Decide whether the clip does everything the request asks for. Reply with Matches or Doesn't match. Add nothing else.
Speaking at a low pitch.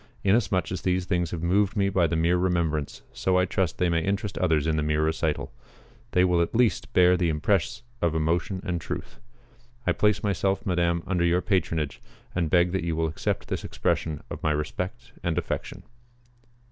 Matches